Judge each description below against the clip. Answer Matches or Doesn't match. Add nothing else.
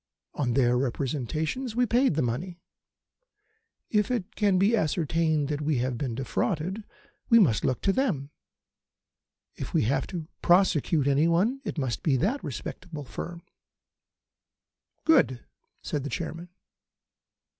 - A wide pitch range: Matches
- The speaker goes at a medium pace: Doesn't match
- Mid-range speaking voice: Matches